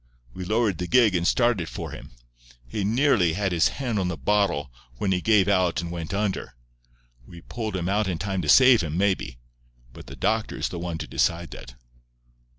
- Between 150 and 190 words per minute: No, average, 200 wpm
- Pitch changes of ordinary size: Yes, average, 3.9 semitones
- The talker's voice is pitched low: Yes, very low, 95 Hz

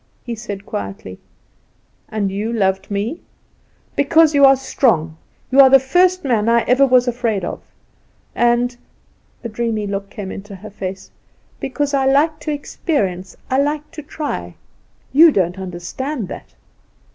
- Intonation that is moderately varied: No, wide, 6.0 semitones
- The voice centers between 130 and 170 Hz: No, high, 240 Hz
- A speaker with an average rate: Yes, average, 150 wpm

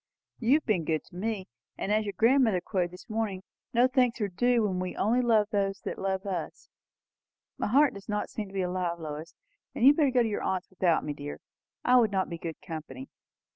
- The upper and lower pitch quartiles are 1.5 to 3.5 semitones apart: No, average, 4.3 semitones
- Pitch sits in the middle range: No, high, 200 Hz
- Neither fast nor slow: No, fast, 220 wpm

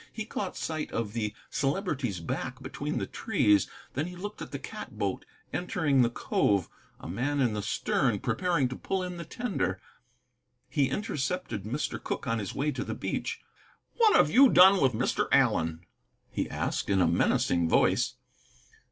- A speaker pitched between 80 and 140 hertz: Yes, low, 135 Hz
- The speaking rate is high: No, average, 170 wpm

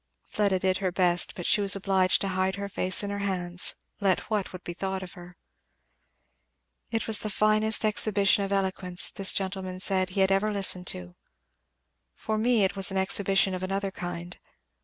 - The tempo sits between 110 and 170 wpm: No, average, 185 wpm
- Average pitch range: No, narrow, 1.5 semitones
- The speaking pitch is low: No, high, 190 Hz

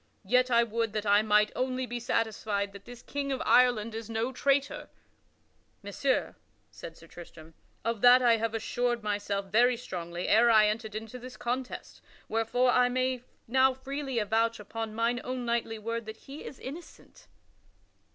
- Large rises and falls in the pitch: No, average, 2.8 semitones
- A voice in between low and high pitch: No, high, 230 Hz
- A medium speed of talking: Yes, average, 165 wpm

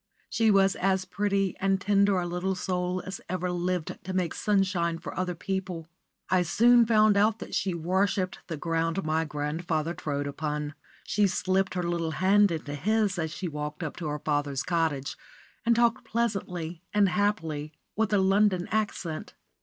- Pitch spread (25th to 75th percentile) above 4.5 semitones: No, average, 3.4 semitones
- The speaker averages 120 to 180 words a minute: Yes, average, 165 wpm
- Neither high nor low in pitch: Yes, medium, 180 Hz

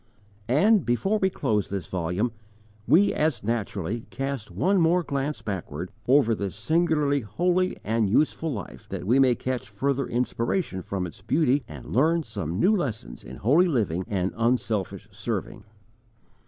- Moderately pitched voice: No, low, 125 Hz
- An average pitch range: No, wide, 7.3 semitones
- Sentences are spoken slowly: No, average, 150 wpm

